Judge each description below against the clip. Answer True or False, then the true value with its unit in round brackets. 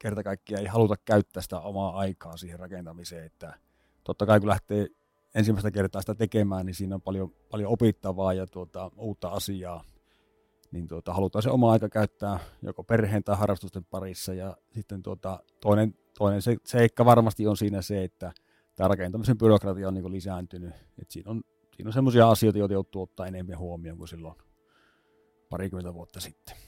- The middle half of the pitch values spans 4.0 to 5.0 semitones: False (2.8 semitones)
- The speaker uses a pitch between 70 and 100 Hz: True (95 Hz)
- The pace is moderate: False (165 wpm)